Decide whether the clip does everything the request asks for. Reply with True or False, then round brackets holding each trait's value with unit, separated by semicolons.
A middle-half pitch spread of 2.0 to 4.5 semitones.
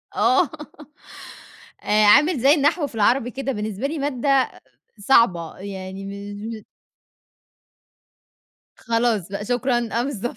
False (5.0 semitones)